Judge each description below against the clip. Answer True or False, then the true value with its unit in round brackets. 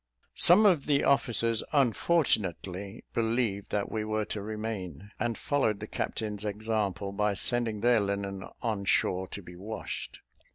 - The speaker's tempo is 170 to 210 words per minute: False (140 wpm)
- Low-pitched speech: True (105 Hz)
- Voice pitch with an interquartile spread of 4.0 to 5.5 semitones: False (2.7 semitones)